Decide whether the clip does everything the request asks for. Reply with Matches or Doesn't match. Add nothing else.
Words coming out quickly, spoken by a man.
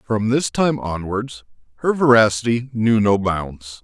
Doesn't match